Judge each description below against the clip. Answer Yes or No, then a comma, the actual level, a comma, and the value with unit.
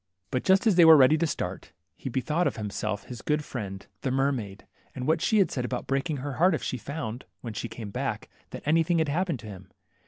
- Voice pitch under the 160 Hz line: Yes, low, 135 Hz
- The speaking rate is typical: No, fast, 230 wpm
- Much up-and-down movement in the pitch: Yes, wide, 5.7 semitones